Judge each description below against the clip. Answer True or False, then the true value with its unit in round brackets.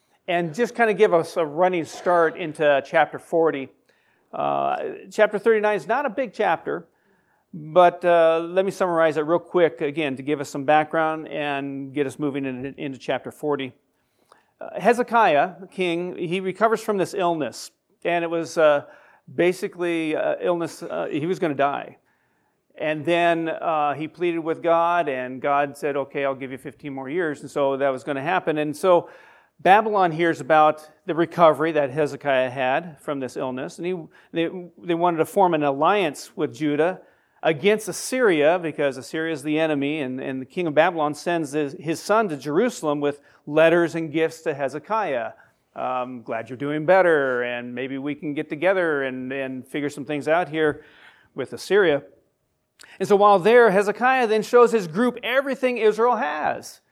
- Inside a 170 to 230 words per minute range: True (180 wpm)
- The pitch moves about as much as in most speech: True (3.9 semitones)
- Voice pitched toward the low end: False (160 Hz)